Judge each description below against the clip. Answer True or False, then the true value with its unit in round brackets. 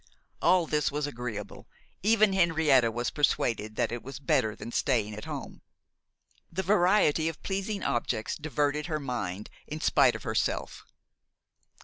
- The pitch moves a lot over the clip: True (6.3 semitones)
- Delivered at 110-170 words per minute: True (140 wpm)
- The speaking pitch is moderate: True (145 Hz)